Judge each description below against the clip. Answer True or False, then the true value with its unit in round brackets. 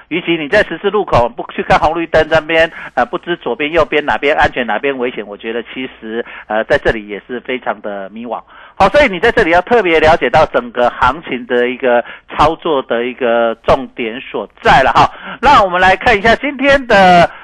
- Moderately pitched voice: True (150 Hz)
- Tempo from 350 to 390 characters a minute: False (305 characters per minute)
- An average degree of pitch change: False (7.6 semitones)